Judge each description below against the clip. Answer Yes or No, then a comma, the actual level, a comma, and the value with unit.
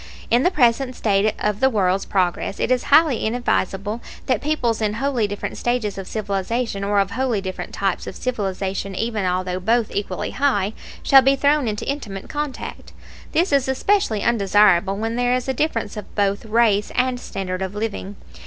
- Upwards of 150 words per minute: Yes, average, 175 wpm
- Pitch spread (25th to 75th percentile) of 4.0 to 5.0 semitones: Yes, average, 4.3 semitones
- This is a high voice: Yes, high, 220 Hz